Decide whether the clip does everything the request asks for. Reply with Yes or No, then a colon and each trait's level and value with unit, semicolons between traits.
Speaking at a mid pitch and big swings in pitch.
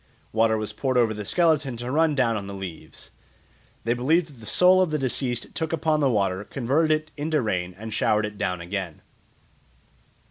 No: low, 120 Hz; wide, 6.5 semitones